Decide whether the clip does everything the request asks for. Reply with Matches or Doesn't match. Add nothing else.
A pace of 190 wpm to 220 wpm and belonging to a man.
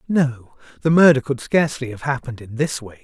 Matches